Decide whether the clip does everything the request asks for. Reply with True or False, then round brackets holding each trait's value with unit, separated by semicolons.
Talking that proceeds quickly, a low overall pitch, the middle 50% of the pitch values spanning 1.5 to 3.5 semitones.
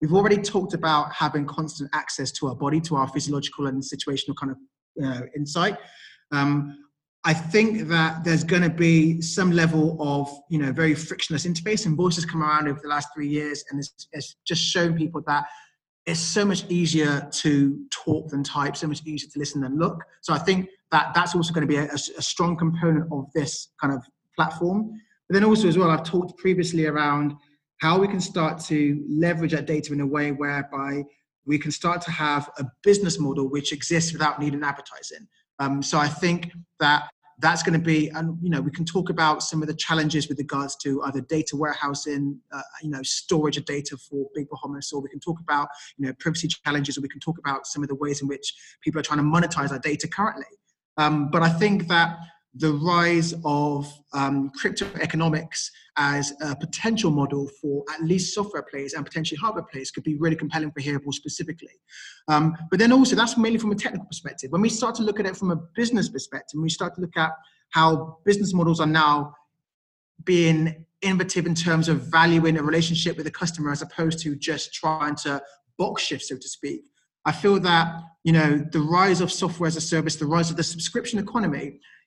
False (210 wpm; 155 Hz; 2.7 semitones)